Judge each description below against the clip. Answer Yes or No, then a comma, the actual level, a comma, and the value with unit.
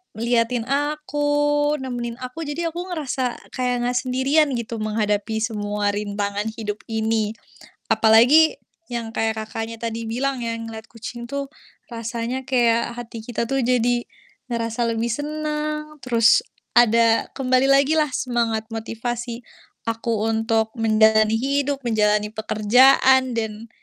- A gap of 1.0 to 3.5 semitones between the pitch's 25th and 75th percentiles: Yes, average, 2.9 semitones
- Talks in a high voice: Yes, high, 235 Hz